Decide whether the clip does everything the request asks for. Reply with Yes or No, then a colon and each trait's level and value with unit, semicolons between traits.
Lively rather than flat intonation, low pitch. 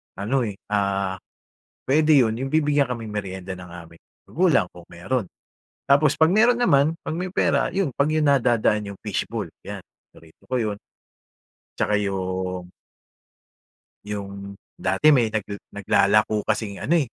Yes: wide, 6.4 semitones; low, 110 Hz